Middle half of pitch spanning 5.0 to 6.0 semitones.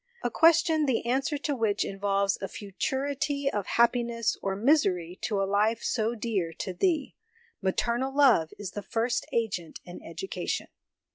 Yes: wide, 5.5 semitones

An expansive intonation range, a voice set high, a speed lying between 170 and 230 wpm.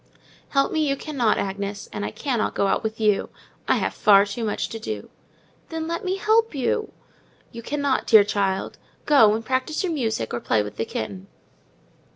Yes: wide, 6.6 semitones; high, 225 Hz; average, 190 wpm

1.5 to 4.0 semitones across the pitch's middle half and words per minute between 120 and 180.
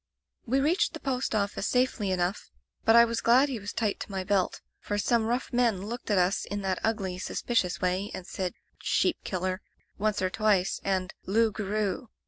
No: average, 3.7 semitones; average, 190 wpm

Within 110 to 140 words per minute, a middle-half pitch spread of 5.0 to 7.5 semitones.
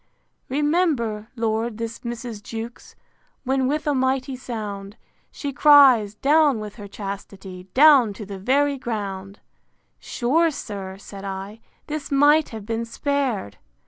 Yes: slow, 135 wpm; wide, 5.4 semitones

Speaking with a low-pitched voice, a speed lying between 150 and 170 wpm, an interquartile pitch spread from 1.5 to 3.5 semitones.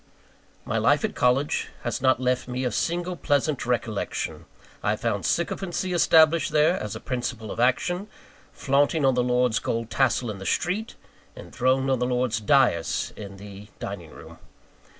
No: low, 125 Hz; average, 160 wpm; average, 4.0 semitones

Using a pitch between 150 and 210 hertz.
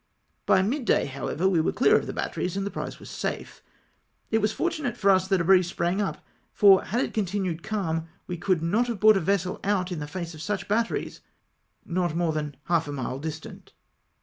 Yes: medium, 185 Hz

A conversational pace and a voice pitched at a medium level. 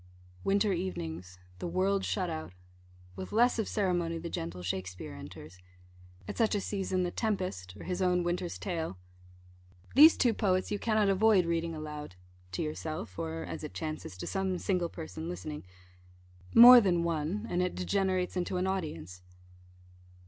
Yes: average, 155 wpm; medium, 180 Hz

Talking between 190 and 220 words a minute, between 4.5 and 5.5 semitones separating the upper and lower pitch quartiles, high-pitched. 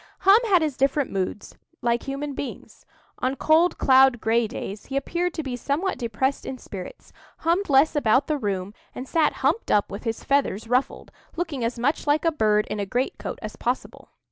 Yes: average, 195 wpm; average, 5.0 semitones; very high, 265 Hz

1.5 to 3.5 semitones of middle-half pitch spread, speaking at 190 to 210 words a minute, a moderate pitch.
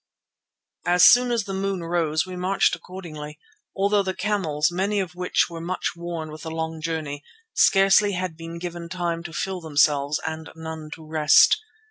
No: average, 2.8 semitones; average, 170 wpm; medium, 170 Hz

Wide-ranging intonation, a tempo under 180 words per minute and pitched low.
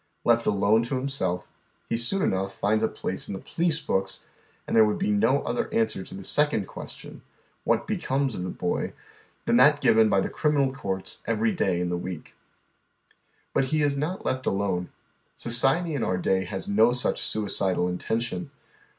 No: wide, 6.3 semitones; average, 185 wpm; low, 110 Hz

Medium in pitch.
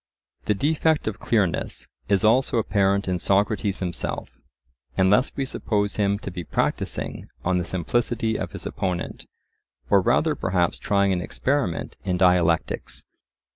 No: low, 100 Hz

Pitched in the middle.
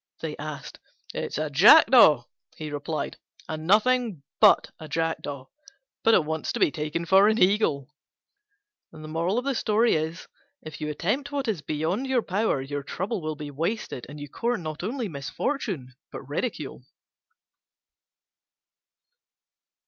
Yes: medium, 165 Hz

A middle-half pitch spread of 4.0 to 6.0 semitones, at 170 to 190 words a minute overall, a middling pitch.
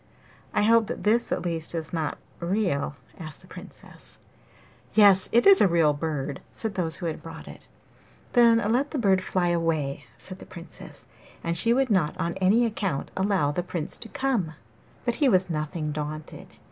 Yes: wide, 5.6 semitones; average, 180 wpm; medium, 180 Hz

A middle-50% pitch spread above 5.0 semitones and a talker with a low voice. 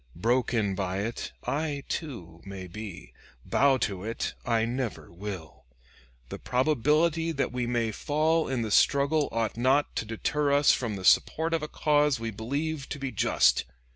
Yes: wide, 5.4 semitones; low, 125 Hz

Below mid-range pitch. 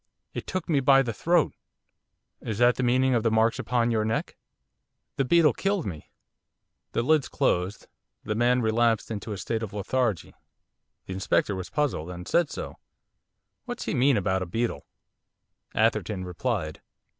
Yes: low, 115 Hz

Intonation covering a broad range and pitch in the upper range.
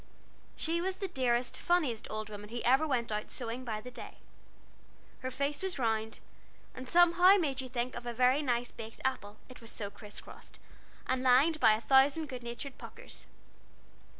No: average, 3.8 semitones; very high, 255 Hz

